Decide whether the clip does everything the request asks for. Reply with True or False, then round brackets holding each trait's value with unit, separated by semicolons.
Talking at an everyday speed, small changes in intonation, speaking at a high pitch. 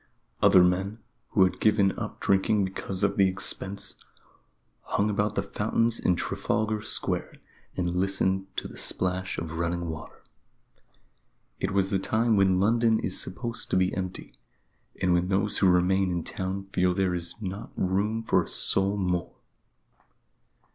False (155 wpm; 2.0 semitones; 95 Hz)